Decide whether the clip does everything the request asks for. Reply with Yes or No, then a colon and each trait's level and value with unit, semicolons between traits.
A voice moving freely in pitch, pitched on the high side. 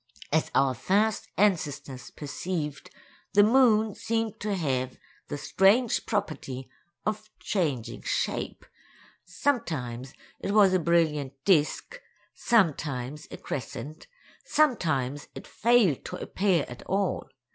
No: wide, 6.9 semitones; medium, 175 Hz